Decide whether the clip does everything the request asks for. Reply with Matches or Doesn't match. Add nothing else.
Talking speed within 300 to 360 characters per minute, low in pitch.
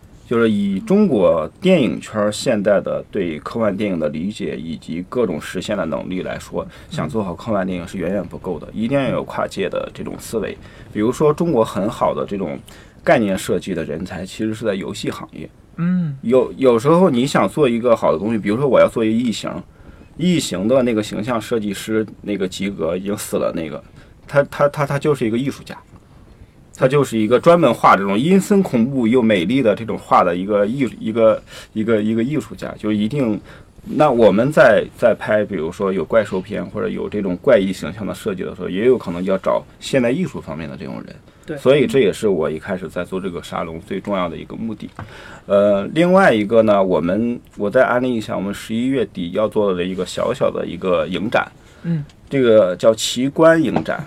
Matches